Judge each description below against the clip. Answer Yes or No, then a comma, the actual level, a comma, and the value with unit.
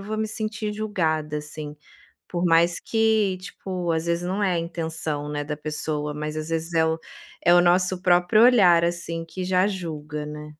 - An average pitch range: Yes, average, 3.3 semitones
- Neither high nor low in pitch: Yes, medium, 170 Hz